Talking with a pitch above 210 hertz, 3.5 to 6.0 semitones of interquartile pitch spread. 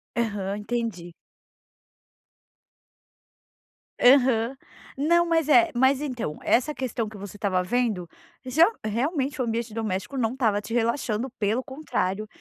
Yes: high, 235 Hz; average, 4.2 semitones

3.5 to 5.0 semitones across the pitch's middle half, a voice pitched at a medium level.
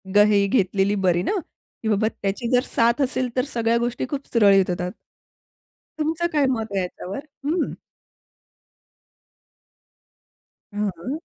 No: average, 4.5 semitones; high, 225 Hz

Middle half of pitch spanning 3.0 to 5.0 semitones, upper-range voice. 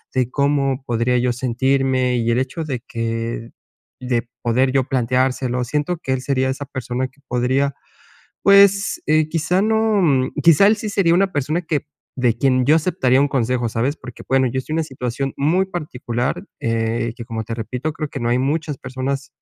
No: average, 3.6 semitones; low, 130 Hz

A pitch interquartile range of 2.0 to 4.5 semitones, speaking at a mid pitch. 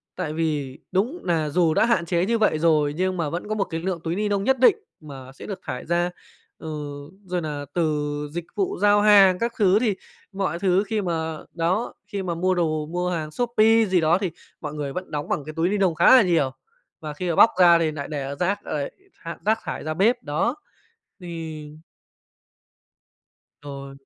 Yes: average, 4.2 semitones; medium, 175 Hz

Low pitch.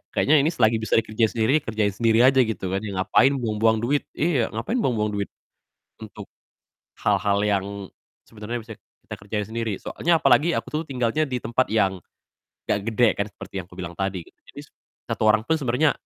Yes: low, 115 Hz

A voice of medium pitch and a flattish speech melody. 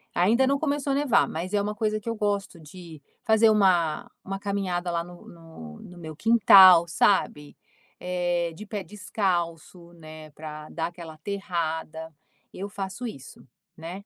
No: medium, 180 Hz; average, 3.8 semitones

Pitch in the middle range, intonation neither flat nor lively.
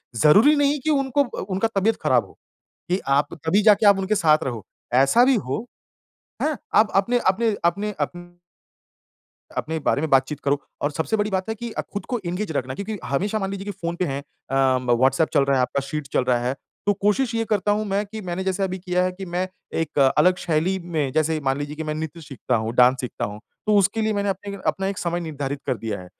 No: medium, 180 Hz; wide, 6.4 semitones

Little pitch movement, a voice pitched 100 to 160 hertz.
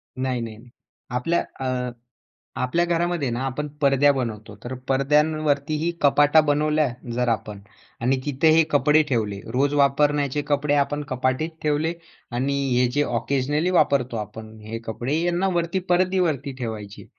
No: average, 3.5 semitones; medium, 140 Hz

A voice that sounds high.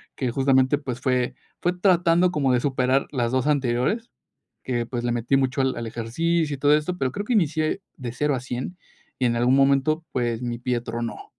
No: low, 130 Hz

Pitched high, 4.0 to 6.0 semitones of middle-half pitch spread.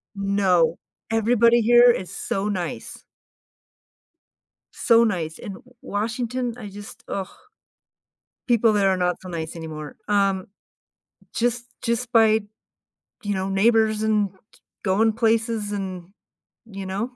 No: high, 205 Hz; average, 3.2 semitones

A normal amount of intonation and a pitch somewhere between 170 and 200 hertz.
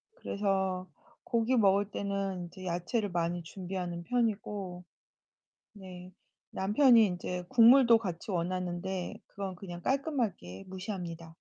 Yes: average, 3.0 semitones; high, 190 Hz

